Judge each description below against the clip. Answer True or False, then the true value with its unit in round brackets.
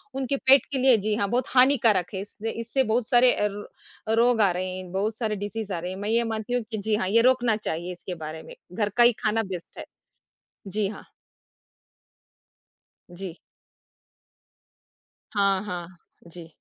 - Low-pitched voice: False (210 Hz)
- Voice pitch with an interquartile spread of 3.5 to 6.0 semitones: True (3.9 semitones)